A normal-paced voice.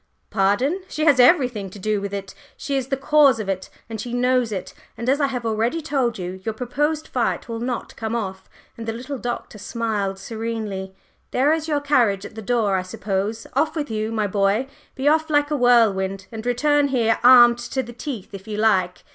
No: fast, 210 wpm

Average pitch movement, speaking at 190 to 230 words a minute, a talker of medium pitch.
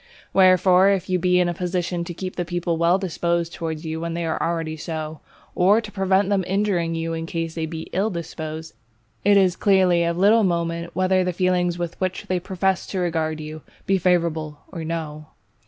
No: narrow, 2.2 semitones; average, 200 wpm; medium, 175 Hz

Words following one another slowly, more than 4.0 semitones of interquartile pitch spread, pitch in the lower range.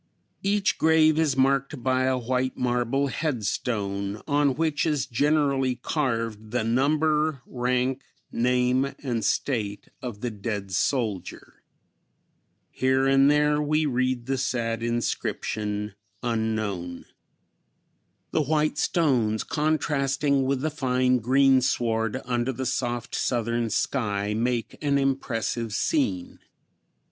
No: slow, 110 wpm; average, 3.5 semitones; low, 130 Hz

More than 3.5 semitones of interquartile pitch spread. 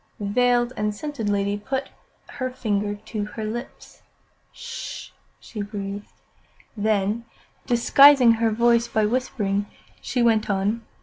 No: average, 2.8 semitones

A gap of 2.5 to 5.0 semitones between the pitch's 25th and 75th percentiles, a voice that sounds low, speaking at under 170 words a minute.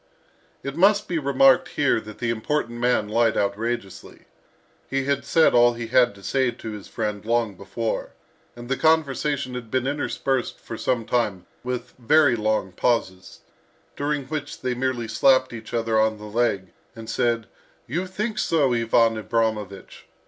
Yes: average, 3.6 semitones; low, 120 Hz; average, 160 wpm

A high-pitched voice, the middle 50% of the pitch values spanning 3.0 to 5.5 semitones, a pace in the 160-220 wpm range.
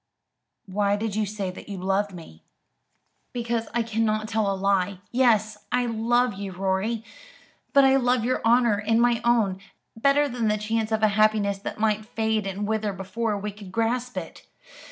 No: high, 215 Hz; narrow, 2.5 semitones; average, 175 wpm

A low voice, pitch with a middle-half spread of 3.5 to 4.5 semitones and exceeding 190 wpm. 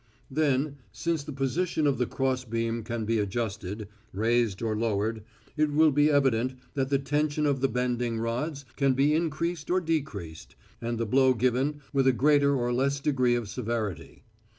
No: low, 130 Hz; average, 3.9 semitones; average, 175 wpm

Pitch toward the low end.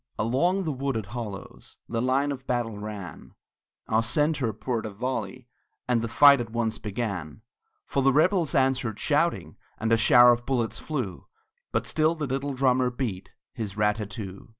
Yes: low, 120 Hz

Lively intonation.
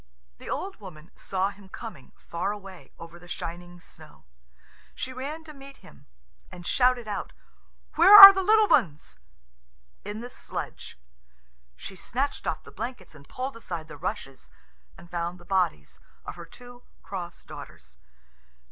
Yes: wide, 6.9 semitones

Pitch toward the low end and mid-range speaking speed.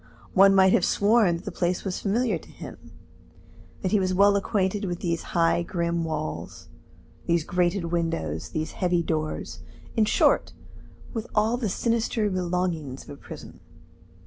No: medium, 180 Hz; average, 155 wpm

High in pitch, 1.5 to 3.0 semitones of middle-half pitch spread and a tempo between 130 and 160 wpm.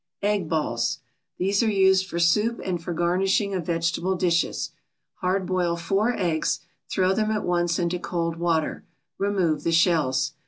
No: medium, 175 Hz; narrow, 2.4 semitones; average, 155 wpm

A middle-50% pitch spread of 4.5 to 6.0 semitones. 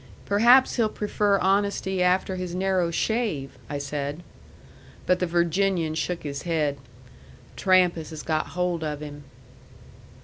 No: average, 3.8 semitones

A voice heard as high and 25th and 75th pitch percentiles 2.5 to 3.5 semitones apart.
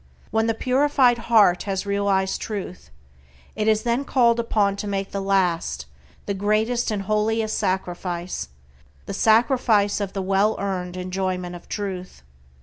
Yes: high, 200 Hz; average, 2.8 semitones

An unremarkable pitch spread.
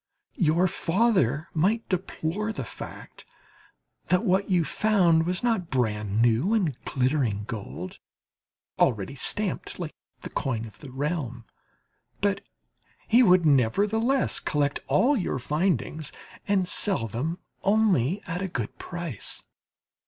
No: wide, 7.3 semitones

